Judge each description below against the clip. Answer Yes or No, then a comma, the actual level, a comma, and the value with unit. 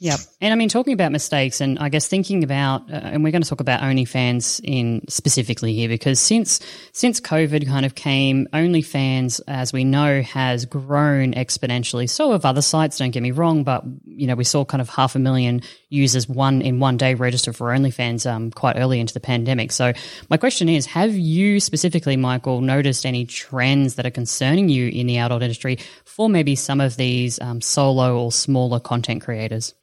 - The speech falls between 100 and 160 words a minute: No, average, 200 wpm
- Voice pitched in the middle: No, low, 130 Hz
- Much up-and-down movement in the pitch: No, average, 2.9 semitones